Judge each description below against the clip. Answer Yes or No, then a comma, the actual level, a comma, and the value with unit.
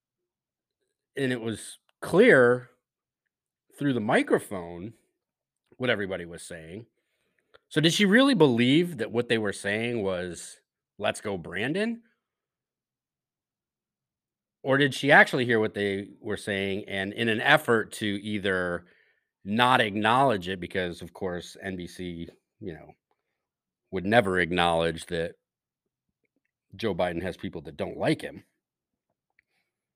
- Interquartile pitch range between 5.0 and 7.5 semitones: Yes, wide, 5.6 semitones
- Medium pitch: No, low, 105 Hz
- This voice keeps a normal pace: No, slow, 120 wpm